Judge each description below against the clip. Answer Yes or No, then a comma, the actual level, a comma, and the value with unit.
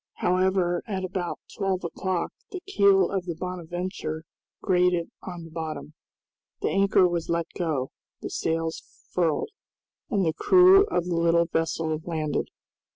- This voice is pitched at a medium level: Yes, medium, 175 Hz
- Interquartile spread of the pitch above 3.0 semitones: No, narrow, 2.4 semitones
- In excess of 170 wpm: No, average, 140 wpm